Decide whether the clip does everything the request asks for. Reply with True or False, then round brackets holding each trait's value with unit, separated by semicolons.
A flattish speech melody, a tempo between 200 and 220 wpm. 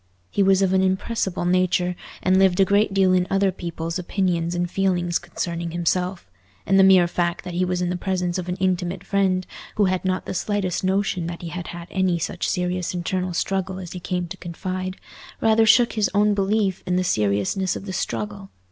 True (1.6 semitones; 205 wpm)